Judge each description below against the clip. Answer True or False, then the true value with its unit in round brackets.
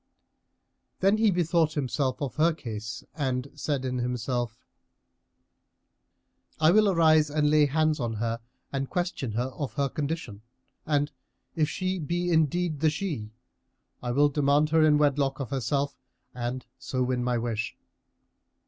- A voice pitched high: False (145 Hz)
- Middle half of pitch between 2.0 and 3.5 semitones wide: False (3.9 semitones)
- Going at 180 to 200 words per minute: False (145 wpm)